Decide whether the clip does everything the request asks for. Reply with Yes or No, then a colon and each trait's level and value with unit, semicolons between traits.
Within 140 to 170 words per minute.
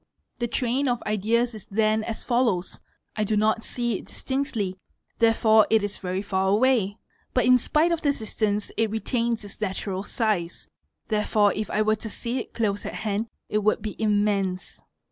No: average, 180 wpm